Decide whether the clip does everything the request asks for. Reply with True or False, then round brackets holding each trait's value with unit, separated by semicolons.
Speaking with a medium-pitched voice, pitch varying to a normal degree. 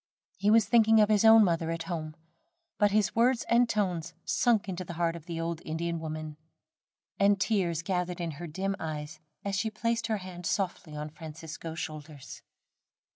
True (175 Hz; 4.3 semitones)